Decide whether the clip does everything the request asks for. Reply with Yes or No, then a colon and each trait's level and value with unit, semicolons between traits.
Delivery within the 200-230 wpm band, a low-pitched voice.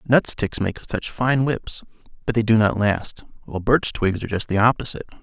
Yes: fast, 205 wpm; low, 110 Hz